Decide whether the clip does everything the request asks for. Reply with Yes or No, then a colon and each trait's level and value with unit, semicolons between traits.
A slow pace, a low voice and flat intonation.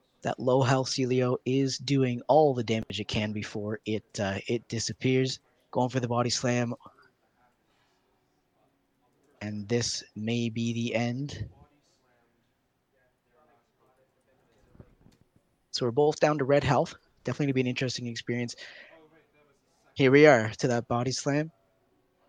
Yes: slow, 125 wpm; low, 125 Hz; narrow, 2.3 semitones